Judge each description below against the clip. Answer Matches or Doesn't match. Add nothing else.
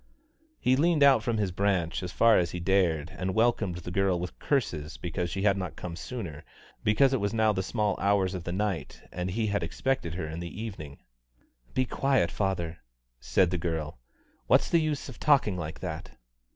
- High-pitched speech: Doesn't match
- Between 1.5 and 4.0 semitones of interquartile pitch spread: Doesn't match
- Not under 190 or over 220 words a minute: Matches